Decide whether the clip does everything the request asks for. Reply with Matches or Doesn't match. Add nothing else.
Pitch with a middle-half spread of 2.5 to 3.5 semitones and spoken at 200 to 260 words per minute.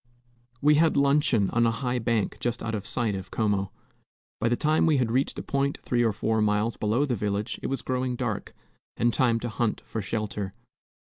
Matches